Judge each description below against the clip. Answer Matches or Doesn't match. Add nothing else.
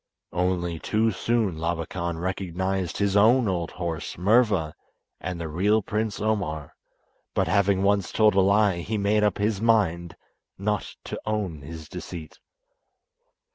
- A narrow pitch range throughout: Doesn't match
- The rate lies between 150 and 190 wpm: Doesn't match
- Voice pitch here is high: Doesn't match